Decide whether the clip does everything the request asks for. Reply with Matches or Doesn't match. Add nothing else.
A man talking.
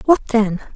Doesn't match